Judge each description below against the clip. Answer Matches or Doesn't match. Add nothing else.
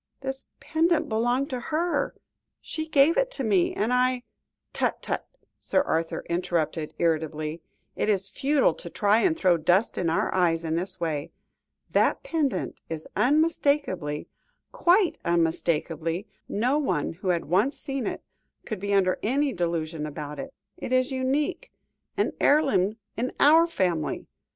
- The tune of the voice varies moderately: Doesn't match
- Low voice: Doesn't match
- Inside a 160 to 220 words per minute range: Doesn't match